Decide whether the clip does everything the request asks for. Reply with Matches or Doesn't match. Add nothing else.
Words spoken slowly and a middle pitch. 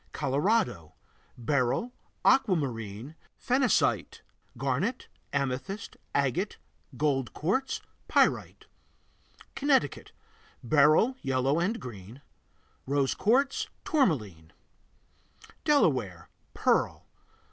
Matches